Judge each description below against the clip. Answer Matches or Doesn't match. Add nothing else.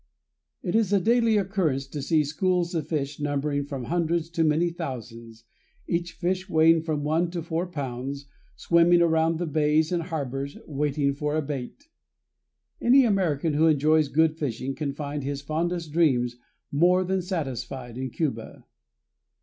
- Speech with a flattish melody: Doesn't match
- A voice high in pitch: Doesn't match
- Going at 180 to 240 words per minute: Doesn't match